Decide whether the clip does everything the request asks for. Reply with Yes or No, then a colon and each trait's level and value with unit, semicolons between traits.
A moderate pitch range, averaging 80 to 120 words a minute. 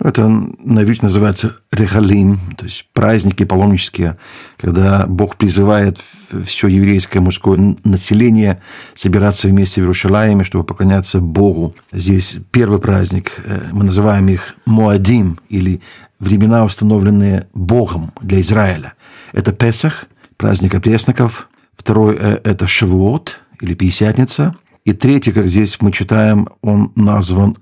No: narrow, 2.2 semitones; average, 115 wpm